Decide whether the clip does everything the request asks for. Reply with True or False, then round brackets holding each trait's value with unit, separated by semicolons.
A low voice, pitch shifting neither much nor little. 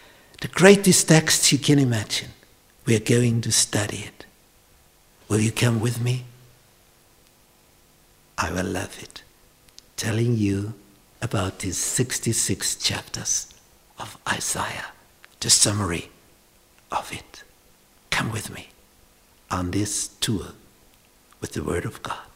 True (115 Hz; 3.8 semitones)